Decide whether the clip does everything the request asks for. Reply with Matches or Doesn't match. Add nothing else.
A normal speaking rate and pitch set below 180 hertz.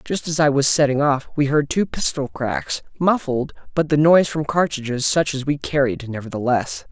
Matches